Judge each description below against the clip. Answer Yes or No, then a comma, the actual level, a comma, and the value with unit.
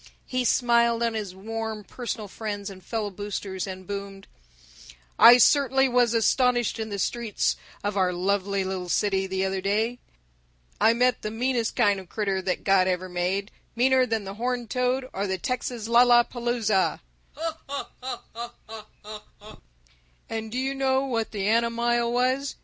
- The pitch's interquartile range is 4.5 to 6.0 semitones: No, average, 3.7 semitones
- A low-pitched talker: No, high, 225 Hz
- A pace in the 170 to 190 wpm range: No, average, 150 wpm